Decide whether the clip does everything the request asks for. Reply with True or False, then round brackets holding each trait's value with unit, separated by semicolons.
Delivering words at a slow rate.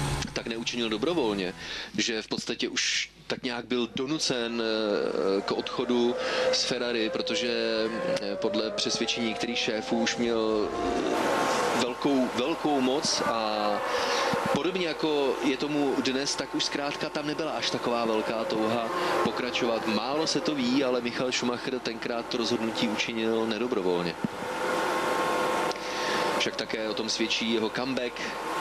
False (125 wpm)